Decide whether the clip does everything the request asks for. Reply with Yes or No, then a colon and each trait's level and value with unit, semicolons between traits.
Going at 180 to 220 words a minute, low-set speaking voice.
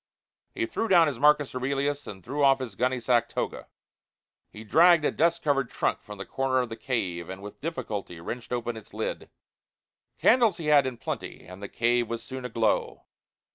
Yes: average, 190 wpm; low, 130 Hz